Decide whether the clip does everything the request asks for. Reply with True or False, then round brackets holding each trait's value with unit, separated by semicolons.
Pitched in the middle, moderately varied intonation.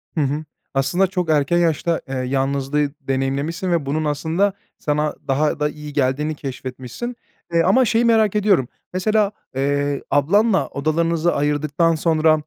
True (155 Hz; 3.6 semitones)